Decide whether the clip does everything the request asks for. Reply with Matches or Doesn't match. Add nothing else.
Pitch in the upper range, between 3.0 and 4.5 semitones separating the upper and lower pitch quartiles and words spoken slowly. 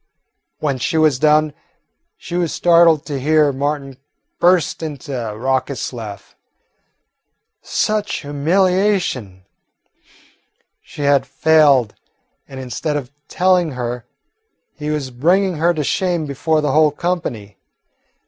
Doesn't match